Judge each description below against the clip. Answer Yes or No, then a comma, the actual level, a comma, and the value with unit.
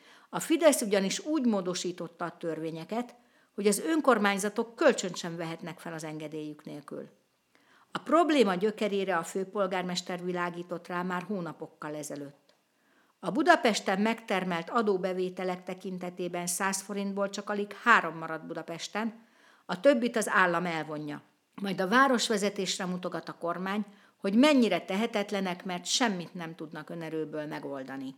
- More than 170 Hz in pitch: Yes, high, 190 Hz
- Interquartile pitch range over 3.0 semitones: Yes, average, 4.1 semitones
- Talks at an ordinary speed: Yes, average, 125 wpm